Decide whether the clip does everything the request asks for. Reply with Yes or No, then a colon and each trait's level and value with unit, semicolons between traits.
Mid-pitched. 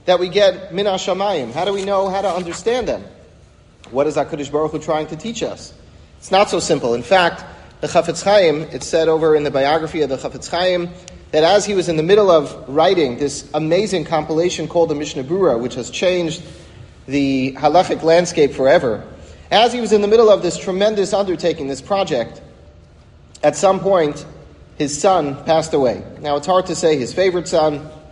Yes: medium, 160 Hz